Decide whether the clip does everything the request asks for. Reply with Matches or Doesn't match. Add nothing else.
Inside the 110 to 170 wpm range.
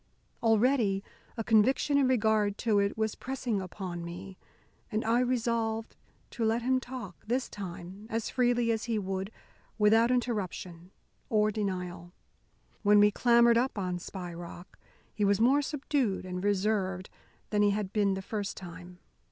Matches